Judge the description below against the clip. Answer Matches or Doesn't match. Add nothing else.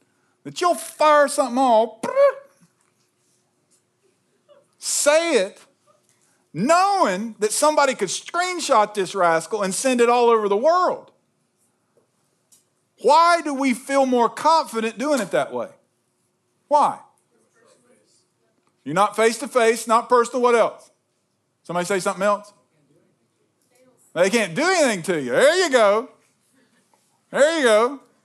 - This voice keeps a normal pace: Doesn't match